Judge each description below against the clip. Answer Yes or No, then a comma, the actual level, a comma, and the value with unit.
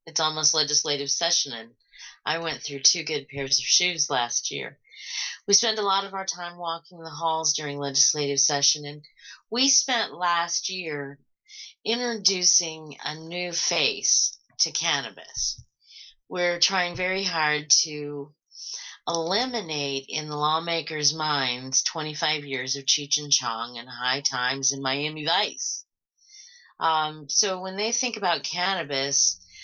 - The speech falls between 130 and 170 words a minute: Yes, average, 140 wpm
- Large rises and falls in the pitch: No, average, 4.0 semitones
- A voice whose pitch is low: No, medium, 155 Hz